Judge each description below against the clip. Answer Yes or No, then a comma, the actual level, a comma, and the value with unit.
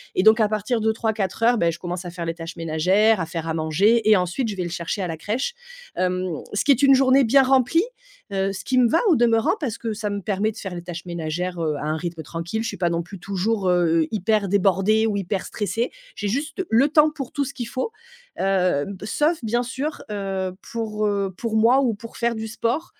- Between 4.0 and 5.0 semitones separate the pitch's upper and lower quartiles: Yes, average, 4.5 semitones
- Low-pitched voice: No, high, 210 Hz